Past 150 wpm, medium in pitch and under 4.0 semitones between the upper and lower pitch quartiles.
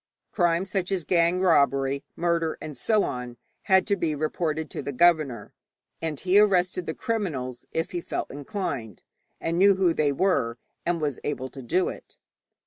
No: average, 170 wpm; medium, 165 Hz; average, 4.7 semitones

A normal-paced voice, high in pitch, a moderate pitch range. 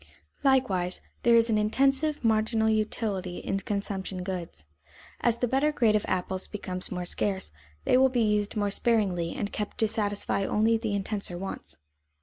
Yes: average, 160 wpm; high, 210 Hz; average, 3.2 semitones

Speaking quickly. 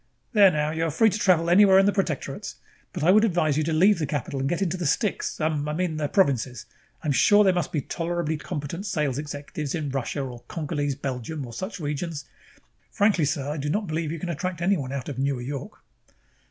Yes: fast, 225 wpm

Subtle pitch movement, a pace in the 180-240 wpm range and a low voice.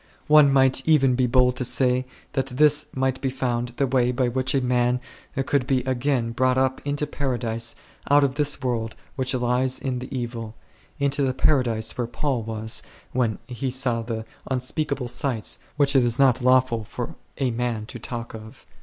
Yes: narrow, 2.0 semitones; average, 185 wpm; low, 130 Hz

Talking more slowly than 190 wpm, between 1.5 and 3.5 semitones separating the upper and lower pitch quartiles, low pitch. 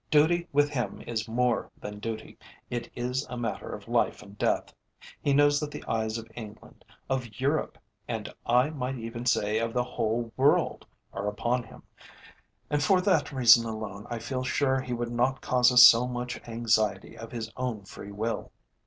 Yes: average, 180 wpm; narrow, 2.6 semitones; low, 120 Hz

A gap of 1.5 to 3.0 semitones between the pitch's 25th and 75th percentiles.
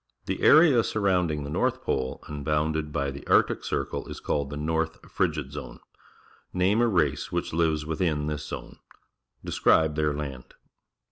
Yes: narrow, 2.6 semitones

